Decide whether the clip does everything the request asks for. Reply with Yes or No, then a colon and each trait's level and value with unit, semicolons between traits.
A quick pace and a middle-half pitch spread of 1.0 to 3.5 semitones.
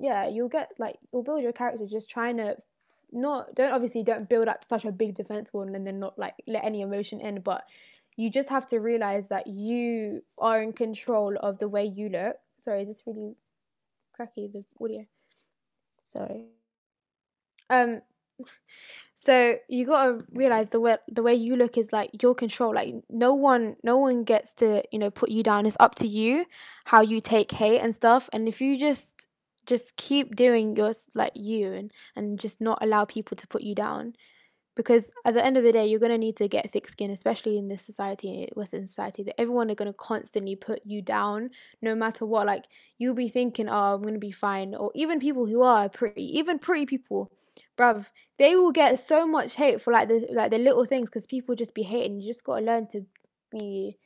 Yes: fast, 210 wpm; average, 2.8 semitones